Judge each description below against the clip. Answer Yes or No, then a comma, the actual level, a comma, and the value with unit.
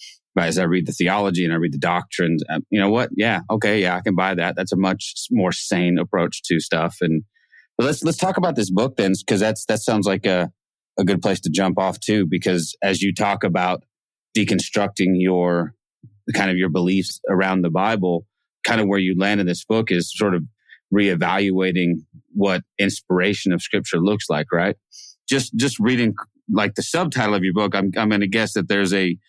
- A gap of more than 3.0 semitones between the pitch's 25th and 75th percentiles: No, narrow, 2.5 semitones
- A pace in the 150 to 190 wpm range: No, fast, 205 wpm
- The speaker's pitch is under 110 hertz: Yes, very low, 95 Hz